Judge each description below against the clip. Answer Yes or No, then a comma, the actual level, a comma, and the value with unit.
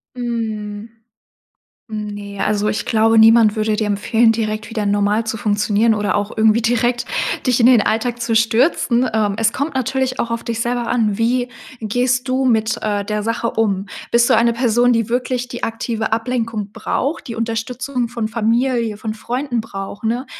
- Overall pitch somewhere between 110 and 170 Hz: No, high, 225 Hz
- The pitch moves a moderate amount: No, narrow, 2.1 semitones